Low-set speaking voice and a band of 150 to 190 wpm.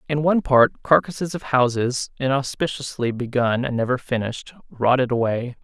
No: low, 130 Hz; average, 140 wpm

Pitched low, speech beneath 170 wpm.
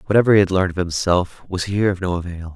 No: very low, 95 Hz; fast, 260 wpm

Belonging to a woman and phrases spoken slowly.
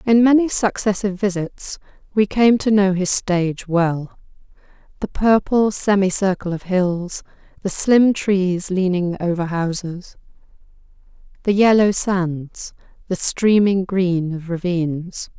Yes: female; slow, 115 wpm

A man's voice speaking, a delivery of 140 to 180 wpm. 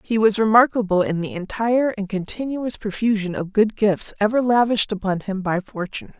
No: female; average, 175 wpm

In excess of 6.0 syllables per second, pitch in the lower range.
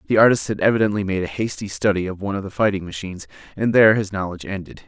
Yes: 7.5 syllables/s; low, 100 Hz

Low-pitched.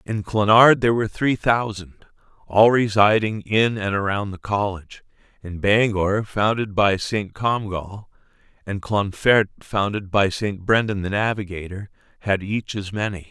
Yes: low, 105 Hz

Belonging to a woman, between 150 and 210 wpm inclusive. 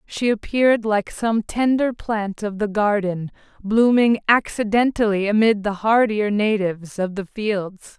No: female; slow, 135 wpm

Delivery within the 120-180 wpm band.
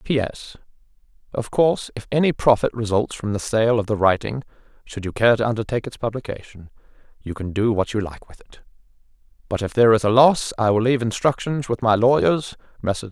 No: average, 190 wpm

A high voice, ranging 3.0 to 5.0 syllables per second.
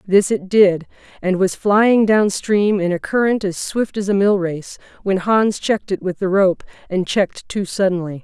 Yes: high, 195 Hz; 4.5 syllables/s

